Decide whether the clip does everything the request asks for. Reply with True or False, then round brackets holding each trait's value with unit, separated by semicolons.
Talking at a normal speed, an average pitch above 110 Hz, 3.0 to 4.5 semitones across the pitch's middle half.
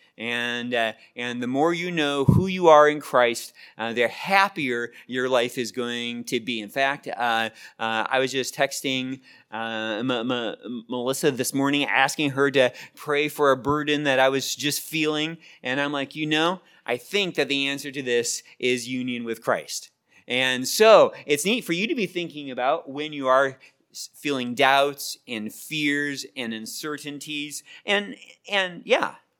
True (175 wpm; 140 Hz; 3.4 semitones)